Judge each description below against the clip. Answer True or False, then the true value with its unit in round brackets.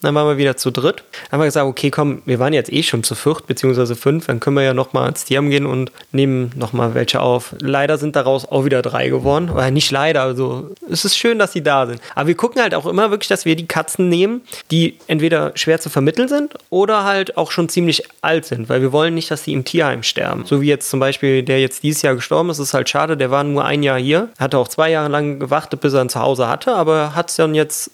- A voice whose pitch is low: False (145 Hz)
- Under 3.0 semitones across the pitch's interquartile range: False (3.5 semitones)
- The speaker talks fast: True (265 wpm)